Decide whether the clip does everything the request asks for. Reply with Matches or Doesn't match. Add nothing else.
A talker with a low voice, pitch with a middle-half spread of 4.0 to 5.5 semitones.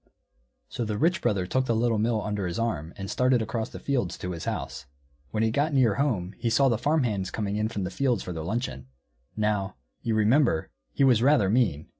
Matches